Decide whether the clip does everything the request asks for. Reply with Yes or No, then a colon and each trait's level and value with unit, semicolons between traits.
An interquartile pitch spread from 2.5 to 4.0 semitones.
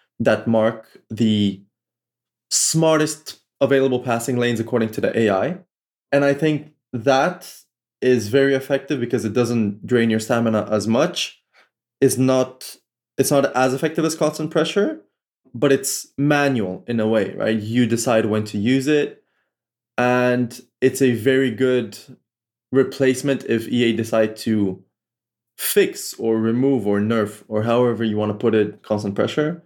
Yes: average, 3.4 semitones